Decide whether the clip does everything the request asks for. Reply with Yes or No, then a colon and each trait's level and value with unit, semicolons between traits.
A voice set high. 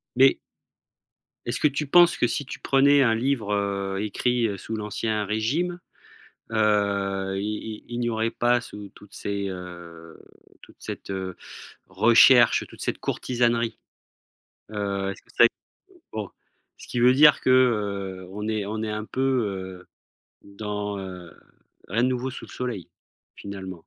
No: low, 105 Hz